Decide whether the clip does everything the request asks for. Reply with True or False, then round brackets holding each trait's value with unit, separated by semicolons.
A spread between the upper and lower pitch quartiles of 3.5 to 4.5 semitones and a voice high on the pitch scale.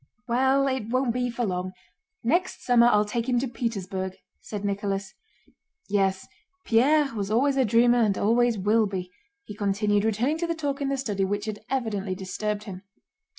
True (3.8 semitones; 220 Hz)